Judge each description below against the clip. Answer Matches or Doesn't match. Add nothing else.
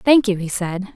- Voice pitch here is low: Doesn't match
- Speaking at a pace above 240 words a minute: Matches